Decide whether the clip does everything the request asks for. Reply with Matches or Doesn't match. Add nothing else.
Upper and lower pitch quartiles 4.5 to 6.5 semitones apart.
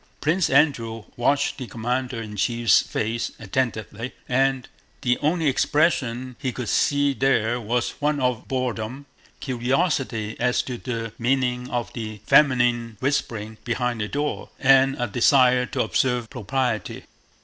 Doesn't match